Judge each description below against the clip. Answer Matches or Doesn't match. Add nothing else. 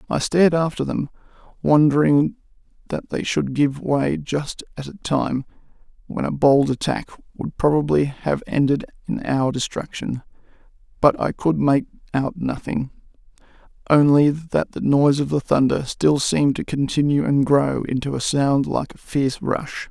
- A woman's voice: Doesn't match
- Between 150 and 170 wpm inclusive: Matches